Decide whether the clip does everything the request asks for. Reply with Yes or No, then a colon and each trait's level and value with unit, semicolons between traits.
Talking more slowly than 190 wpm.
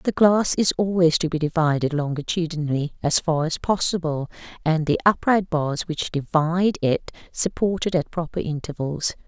Yes: average, 150 wpm